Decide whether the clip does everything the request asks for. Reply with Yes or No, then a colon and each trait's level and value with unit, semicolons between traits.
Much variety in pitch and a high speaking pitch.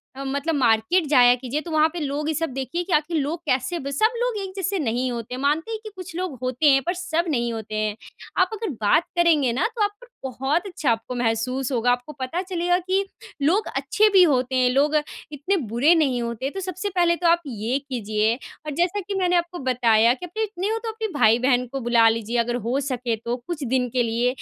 Yes: wide, 6.2 semitones; very high, 280 Hz